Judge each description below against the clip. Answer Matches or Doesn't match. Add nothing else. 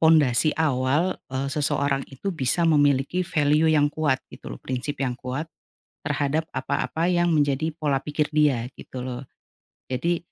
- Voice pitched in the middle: Matches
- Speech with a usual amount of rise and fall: Matches